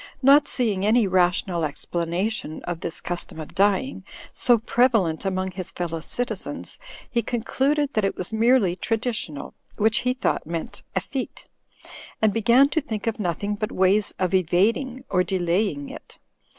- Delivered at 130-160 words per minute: Yes, average, 150 wpm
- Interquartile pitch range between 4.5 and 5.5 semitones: Yes, average, 5.1 semitones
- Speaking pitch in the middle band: No, high, 205 Hz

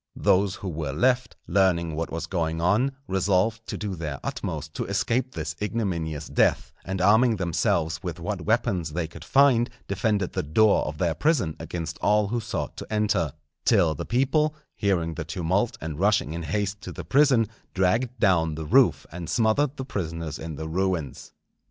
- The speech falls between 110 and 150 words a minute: No, average, 175 wpm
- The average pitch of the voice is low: Yes, very low, 95 Hz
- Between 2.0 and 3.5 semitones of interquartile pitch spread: No, average, 5.1 semitones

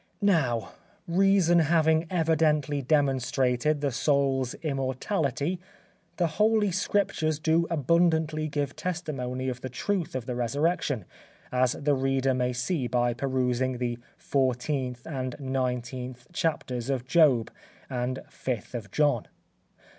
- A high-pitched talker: No, low, 135 Hz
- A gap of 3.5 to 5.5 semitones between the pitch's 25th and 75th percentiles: Yes, average, 4.1 semitones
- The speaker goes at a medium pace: No, slow, 115 wpm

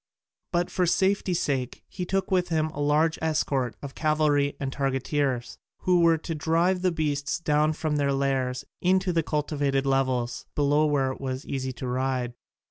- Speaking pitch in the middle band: Yes, medium, 145 Hz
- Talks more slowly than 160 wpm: No, average, 170 wpm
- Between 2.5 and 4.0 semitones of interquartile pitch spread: Yes, average, 3.4 semitones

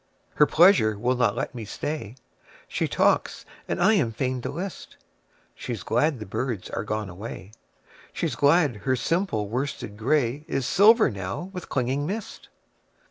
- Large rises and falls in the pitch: Yes, wide, 6.3 semitones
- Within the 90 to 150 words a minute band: Yes, slow, 135 wpm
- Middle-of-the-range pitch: No, low, 130 Hz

